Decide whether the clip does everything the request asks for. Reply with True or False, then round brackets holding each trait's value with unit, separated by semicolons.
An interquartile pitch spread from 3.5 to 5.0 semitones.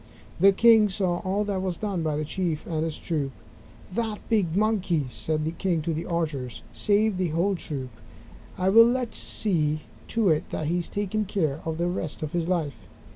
True (4.3 semitones)